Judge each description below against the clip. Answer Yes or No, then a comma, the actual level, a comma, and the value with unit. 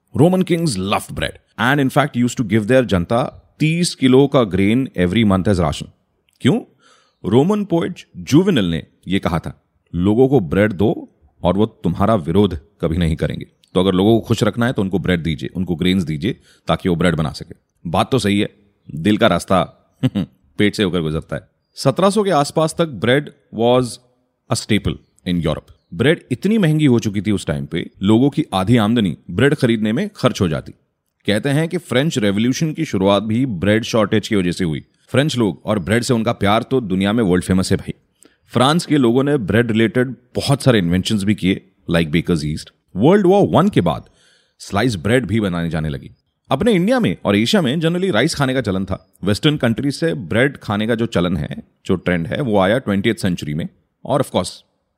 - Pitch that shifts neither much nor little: No, wide, 6.0 semitones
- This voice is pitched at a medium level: No, low, 110 Hz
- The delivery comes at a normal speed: No, fast, 200 wpm